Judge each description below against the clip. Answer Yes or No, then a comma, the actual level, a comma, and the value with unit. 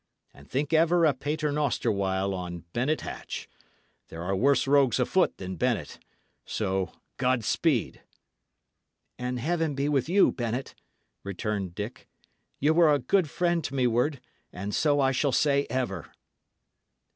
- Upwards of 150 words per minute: No, average, 145 wpm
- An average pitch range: No, wide, 6.4 semitones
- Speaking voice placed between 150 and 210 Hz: No, low, 130 Hz